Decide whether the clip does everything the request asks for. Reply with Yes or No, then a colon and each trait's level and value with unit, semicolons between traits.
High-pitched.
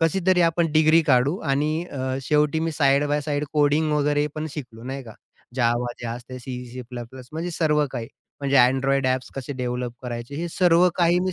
No: medium, 145 Hz